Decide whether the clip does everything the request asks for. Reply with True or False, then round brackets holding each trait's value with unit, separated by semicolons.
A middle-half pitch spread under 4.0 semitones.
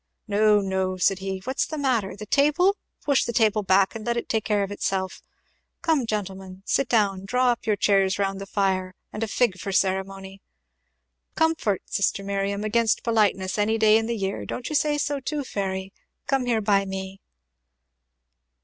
True (3.5 semitones)